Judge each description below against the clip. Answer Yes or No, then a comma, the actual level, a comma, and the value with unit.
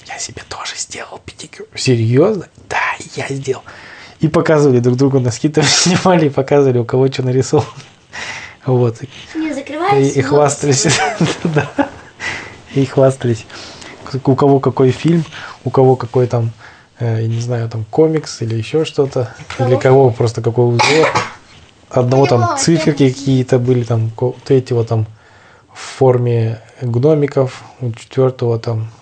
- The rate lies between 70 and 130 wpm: Yes, average, 125 wpm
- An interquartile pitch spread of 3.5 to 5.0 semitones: No, average, 2.9 semitones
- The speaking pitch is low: Yes, low, 130 Hz